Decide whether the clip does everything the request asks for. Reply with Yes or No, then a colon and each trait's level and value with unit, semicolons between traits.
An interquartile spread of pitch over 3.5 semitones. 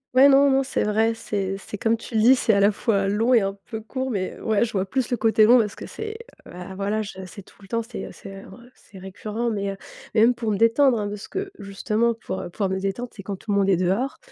No: average, 3.1 semitones